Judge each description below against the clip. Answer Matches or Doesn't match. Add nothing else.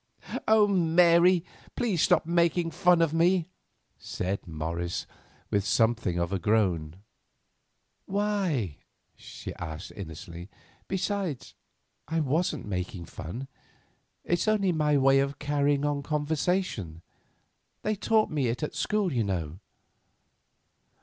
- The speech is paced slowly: Matches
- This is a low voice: Doesn't match